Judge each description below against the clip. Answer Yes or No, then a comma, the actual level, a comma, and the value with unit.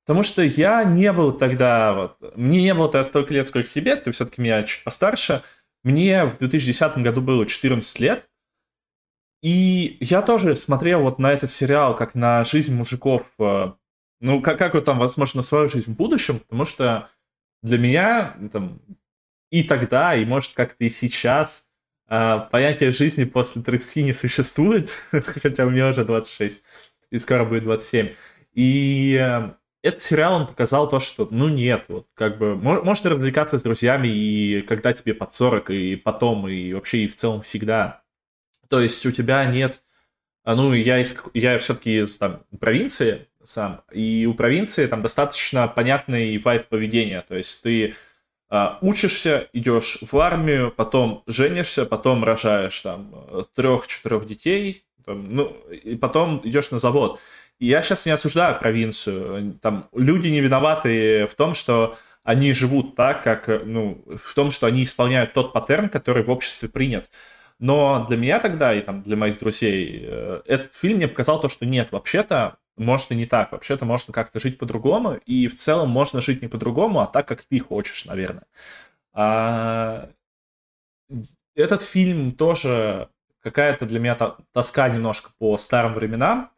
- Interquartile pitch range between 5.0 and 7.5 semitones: No, average, 4.2 semitones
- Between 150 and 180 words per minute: Yes, fast, 160 wpm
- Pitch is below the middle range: Yes, low, 125 Hz